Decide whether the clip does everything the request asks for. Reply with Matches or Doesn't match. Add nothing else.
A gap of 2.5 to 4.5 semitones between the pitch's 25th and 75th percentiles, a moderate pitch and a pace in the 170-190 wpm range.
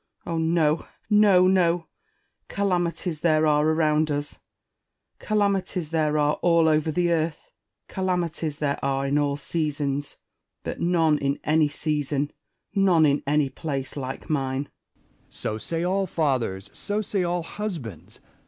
Doesn't match